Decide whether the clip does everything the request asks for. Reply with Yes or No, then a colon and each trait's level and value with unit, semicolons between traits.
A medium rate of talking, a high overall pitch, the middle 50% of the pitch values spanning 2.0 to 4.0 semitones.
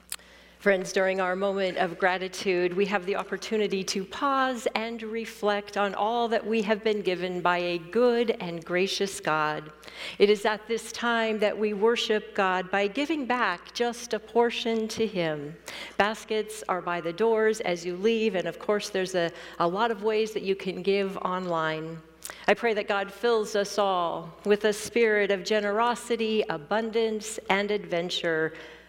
Yes: average, 170 wpm; high, 205 Hz; average, 3.4 semitones